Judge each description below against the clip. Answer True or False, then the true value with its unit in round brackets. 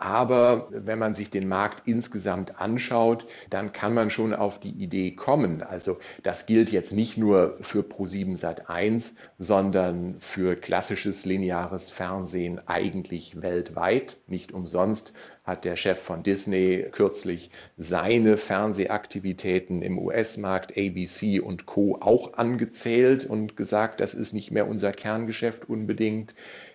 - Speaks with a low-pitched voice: True (100 Hz)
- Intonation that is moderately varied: True (3.0 semitones)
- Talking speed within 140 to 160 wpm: False (130 wpm)